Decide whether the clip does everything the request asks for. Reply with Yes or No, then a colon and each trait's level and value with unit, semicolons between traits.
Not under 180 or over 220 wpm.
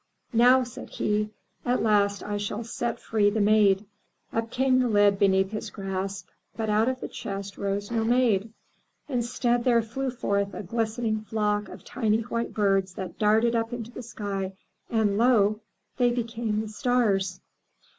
No: average, 165 wpm